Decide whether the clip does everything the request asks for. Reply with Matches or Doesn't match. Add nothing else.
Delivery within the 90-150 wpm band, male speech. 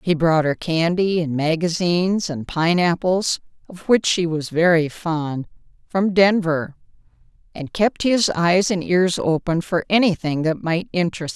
Doesn't match